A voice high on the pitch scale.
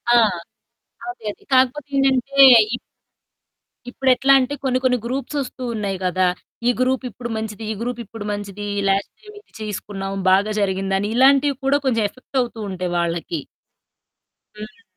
Yes: high, 235 Hz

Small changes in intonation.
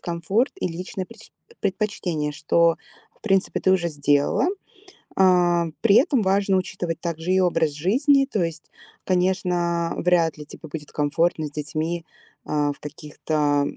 No: average, 3.4 semitones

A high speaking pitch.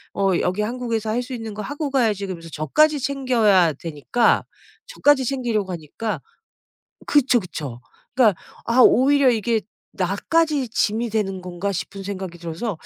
Yes: high, 220 Hz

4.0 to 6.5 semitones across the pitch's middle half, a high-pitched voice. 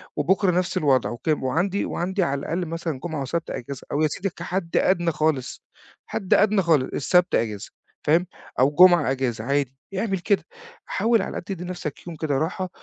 No: average, 4.6 semitones; medium, 165 Hz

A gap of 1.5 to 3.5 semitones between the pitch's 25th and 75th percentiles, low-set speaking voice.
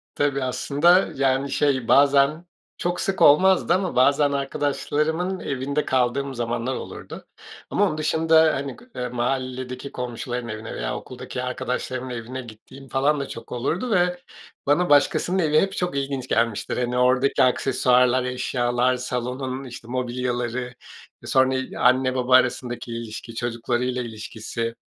Yes: narrow, 2.6 semitones; low, 130 Hz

